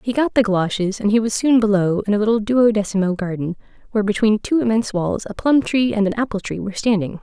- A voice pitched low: No, high, 215 Hz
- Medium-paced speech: No, fast, 225 wpm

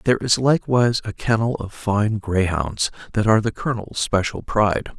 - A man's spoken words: Yes, male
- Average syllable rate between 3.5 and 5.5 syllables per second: Yes, 5.4 syllables/s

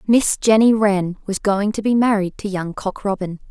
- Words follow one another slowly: No, fast, 205 wpm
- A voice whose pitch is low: No, high, 205 Hz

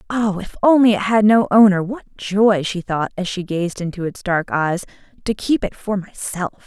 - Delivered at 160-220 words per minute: Yes, fast, 205 wpm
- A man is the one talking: No, female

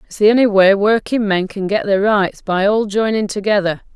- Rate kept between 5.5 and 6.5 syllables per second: No, 5.1 syllables/s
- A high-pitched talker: Yes, high, 205 Hz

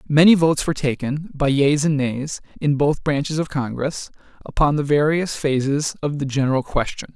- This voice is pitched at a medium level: Yes, medium, 145 Hz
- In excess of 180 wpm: No, average, 175 wpm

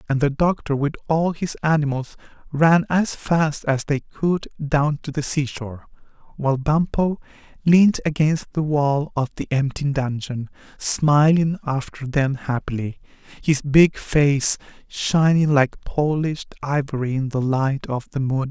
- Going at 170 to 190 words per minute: No, average, 145 wpm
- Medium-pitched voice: Yes, medium, 145 Hz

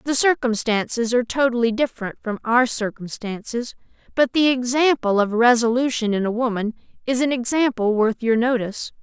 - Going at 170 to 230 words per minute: No, average, 145 wpm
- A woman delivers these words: Yes, female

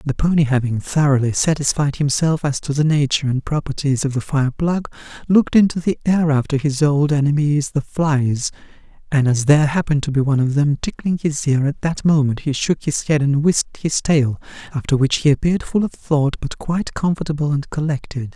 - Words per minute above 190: Yes, average, 200 wpm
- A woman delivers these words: No, male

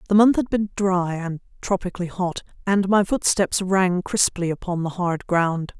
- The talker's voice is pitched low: No, medium, 185 Hz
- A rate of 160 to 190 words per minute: Yes, average, 175 wpm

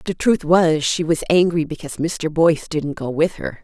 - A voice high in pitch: No, medium, 160 Hz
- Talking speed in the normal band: No, fast, 215 wpm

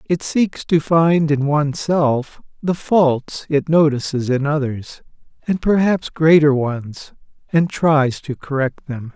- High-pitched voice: No, medium, 150 Hz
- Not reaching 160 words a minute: Yes, average, 140 wpm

